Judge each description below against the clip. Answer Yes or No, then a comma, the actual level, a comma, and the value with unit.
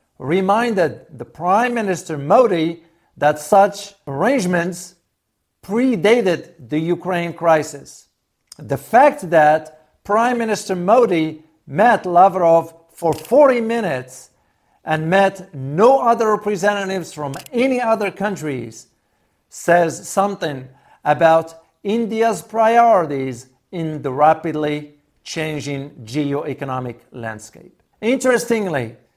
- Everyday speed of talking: No, slow, 90 wpm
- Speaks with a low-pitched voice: No, medium, 165 Hz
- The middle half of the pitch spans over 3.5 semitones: Yes, wide, 5.6 semitones